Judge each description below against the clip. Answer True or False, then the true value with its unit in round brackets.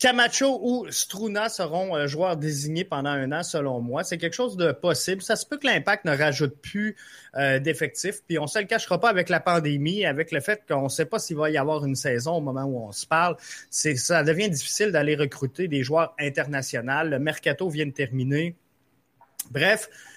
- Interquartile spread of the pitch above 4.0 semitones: True (4.6 semitones)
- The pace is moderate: True (205 wpm)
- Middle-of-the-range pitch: True (160 Hz)